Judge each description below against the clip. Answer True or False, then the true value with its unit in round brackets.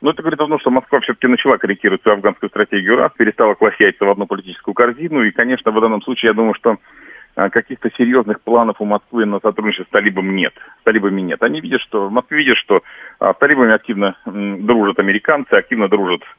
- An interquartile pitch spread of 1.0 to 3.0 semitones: False (3.8 semitones)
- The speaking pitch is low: True (115 Hz)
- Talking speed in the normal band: False (200 wpm)